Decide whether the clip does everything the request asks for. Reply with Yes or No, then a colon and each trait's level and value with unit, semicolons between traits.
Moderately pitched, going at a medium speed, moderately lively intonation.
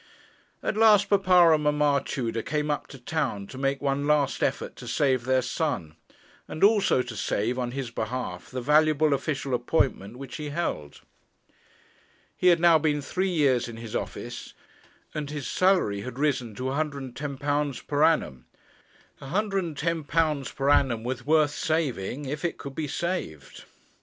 Yes: medium, 145 Hz; average, 155 wpm; average, 3.8 semitones